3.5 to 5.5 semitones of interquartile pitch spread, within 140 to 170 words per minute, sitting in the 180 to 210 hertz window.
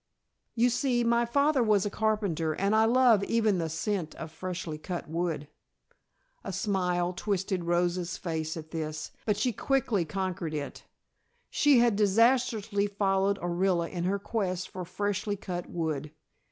Yes: average, 4.1 semitones; average, 150 wpm; high, 190 Hz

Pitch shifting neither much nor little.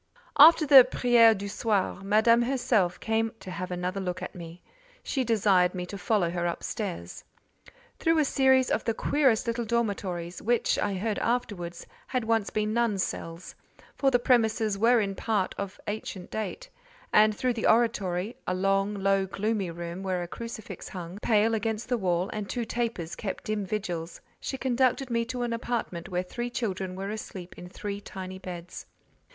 Yes: average, 4.3 semitones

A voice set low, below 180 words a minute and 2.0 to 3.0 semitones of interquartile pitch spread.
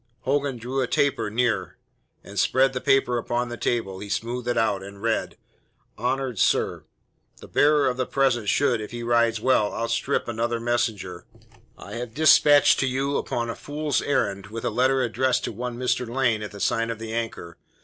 No: low, 120 Hz; average, 190 wpm; narrow, 2.6 semitones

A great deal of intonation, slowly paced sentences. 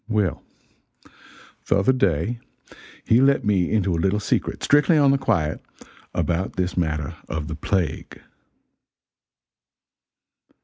Yes: wide, 5.8 semitones; slow, 120 wpm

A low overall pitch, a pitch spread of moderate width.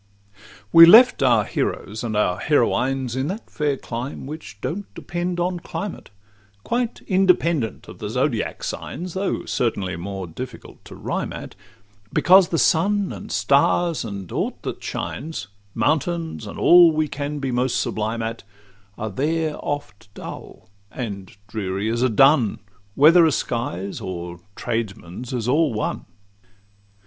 No: low, 130 Hz; wide, 7.2 semitones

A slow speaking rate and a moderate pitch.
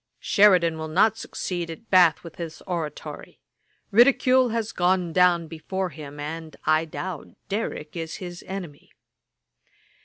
Yes: slow, 130 wpm; medium, 175 Hz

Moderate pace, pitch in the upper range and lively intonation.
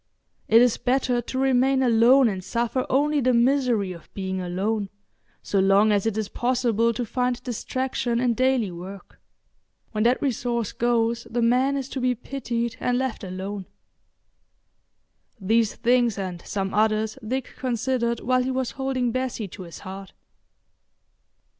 No: average, 150 wpm; high, 235 Hz; average, 3.4 semitones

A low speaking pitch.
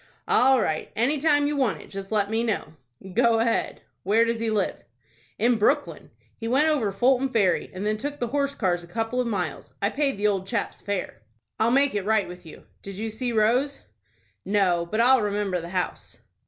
No: high, 220 Hz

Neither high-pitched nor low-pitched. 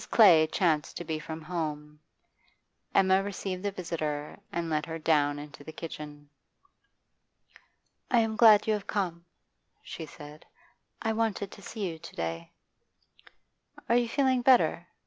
Yes: medium, 170 Hz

